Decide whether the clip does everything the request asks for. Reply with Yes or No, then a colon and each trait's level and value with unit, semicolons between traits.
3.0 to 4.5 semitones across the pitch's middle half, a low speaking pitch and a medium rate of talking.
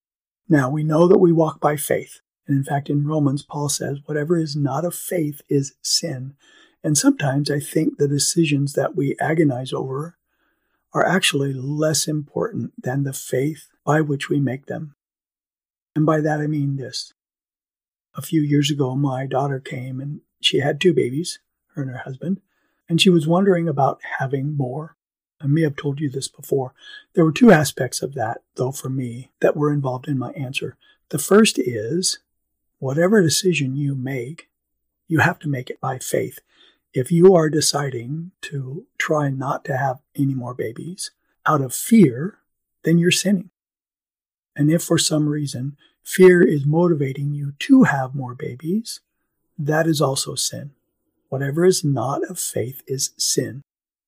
No: average, 3.5 semitones; medium, 150 Hz; average, 170 wpm